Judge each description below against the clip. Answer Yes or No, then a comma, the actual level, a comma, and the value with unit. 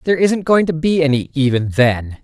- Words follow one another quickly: Yes, fast, 215 wpm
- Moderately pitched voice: Yes, medium, 150 Hz